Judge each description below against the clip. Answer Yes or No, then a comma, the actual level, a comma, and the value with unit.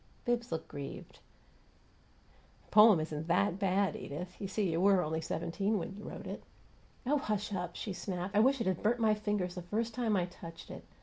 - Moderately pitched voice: No, high, 195 Hz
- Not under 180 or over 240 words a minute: Yes, average, 200 wpm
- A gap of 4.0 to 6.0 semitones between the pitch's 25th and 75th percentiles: No, average, 3.5 semitones